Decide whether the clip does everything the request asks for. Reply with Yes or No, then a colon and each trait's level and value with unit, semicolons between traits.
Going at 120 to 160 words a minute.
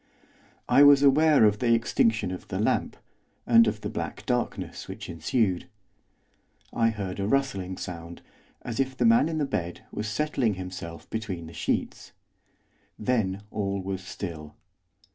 Yes: average, 150 wpm